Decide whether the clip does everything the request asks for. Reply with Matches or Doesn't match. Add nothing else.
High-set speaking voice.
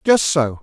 Doesn't match